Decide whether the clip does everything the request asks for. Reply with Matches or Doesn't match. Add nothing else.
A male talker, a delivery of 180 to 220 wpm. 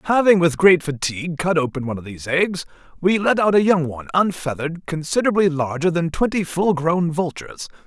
Matches